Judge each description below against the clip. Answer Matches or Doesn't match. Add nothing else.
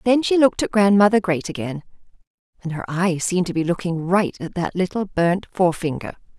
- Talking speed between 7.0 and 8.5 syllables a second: Doesn't match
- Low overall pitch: Doesn't match